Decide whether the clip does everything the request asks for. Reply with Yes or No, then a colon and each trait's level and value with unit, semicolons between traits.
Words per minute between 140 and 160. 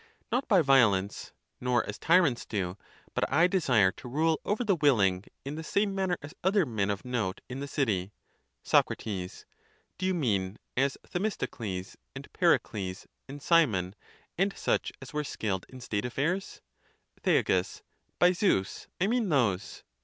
Yes: average, 155 wpm